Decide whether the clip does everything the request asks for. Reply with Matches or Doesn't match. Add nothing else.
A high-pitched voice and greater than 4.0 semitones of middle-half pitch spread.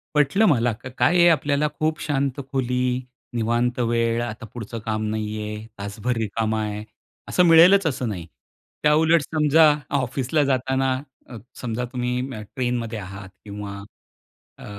Doesn't match